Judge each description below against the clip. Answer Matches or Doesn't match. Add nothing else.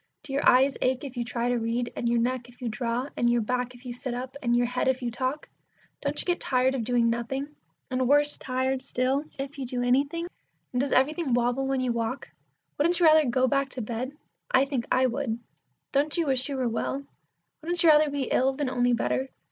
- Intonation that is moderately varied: Doesn't match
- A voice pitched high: Matches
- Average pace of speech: Doesn't match